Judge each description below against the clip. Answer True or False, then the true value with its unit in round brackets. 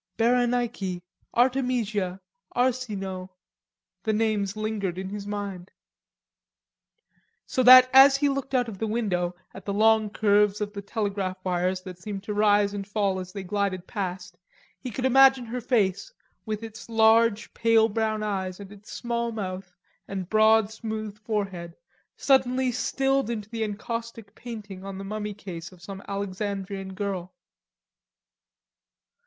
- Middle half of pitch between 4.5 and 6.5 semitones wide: False (3.0 semitones)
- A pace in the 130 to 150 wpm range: True (140 wpm)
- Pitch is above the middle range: True (210 Hz)